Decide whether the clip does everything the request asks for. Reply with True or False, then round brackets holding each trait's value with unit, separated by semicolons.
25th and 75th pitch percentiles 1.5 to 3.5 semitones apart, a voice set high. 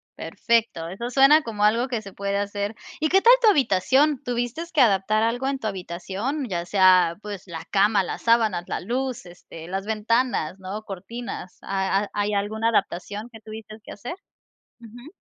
False (3.9 semitones; 215 Hz)